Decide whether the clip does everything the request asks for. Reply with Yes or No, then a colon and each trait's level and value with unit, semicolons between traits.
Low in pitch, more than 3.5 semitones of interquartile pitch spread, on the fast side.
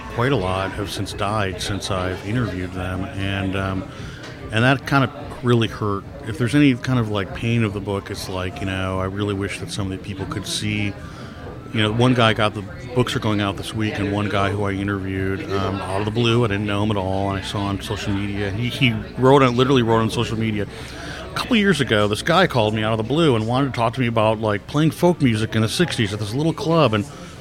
Yes: low, 105 Hz; average, 3.9 semitones; fast, 265 wpm